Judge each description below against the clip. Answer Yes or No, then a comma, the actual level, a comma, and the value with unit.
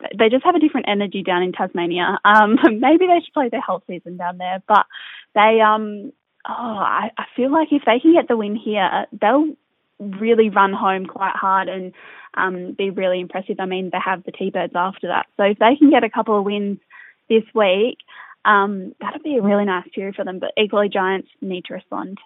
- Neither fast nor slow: No, fast, 215 wpm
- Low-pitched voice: No, high, 205 Hz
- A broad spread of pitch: No, average, 3.2 semitones